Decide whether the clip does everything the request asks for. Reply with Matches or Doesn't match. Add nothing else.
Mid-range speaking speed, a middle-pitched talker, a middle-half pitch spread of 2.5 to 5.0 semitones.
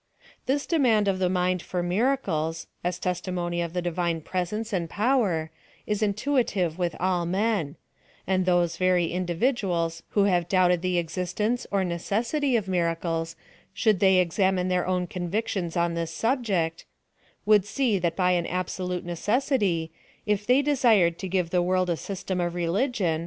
Matches